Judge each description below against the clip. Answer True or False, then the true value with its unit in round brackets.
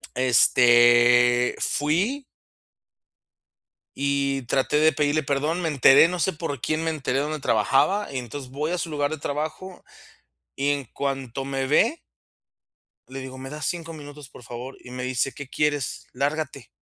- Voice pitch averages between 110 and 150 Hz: True (140 Hz)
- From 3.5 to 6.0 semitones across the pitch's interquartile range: False (3.0 semitones)